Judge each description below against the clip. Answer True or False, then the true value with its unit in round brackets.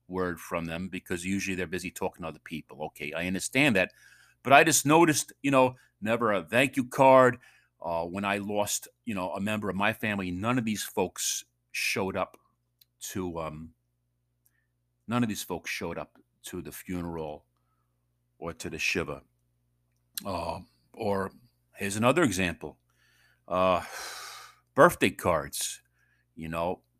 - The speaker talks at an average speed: True (150 wpm)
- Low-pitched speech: True (90 Hz)